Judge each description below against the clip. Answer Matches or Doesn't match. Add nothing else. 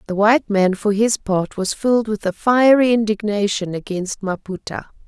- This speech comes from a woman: Matches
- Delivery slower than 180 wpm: Matches